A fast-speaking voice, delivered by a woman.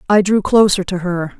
Yes: fast, 215 wpm; female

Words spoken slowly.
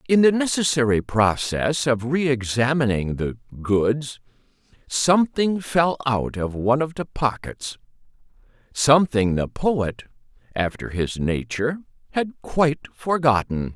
Yes: slow, 115 wpm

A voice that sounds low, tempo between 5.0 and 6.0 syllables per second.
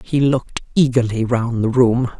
No: low, 120 Hz; 4.6 syllables/s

